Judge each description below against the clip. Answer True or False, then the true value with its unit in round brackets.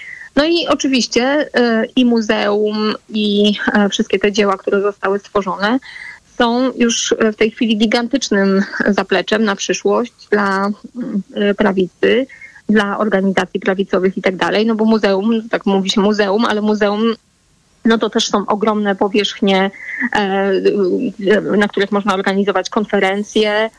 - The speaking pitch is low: False (210 Hz)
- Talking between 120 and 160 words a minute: True (140 wpm)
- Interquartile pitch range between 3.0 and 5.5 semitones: False (2.4 semitones)